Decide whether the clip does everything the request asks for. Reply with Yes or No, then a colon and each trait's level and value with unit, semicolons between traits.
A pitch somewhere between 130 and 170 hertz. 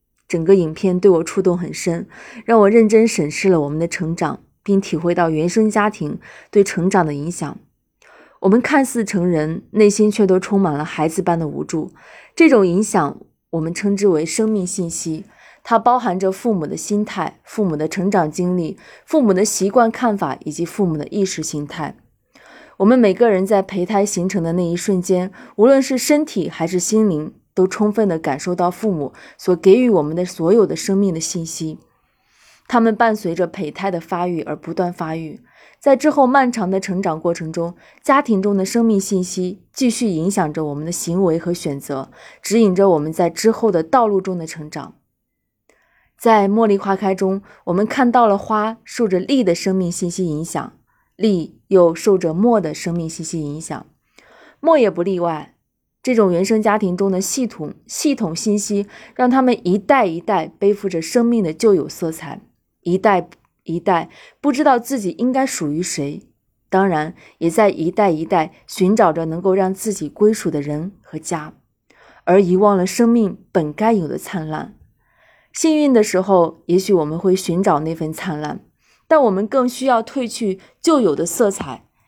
No: high, 190 Hz